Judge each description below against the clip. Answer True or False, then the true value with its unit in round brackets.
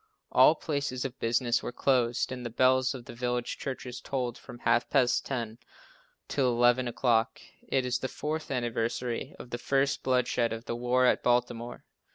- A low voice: True (125 Hz)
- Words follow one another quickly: False (175 wpm)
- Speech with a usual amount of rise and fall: False (1.4 semitones)